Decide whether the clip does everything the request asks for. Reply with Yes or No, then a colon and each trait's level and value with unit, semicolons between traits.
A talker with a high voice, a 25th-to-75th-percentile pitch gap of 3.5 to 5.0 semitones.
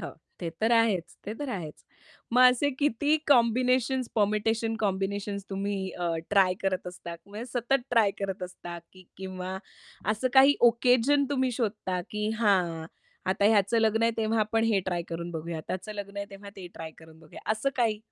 Yes: high, 210 Hz; average, 3.8 semitones